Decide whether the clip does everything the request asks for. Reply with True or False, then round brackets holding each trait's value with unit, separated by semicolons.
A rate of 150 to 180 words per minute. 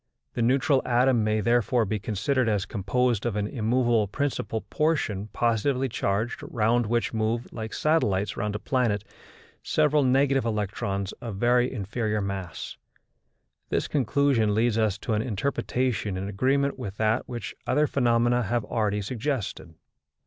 False (140 wpm)